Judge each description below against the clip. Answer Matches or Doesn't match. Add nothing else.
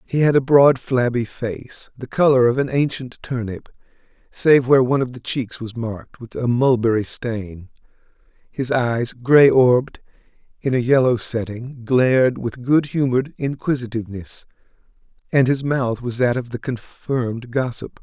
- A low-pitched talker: Matches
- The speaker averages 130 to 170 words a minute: Matches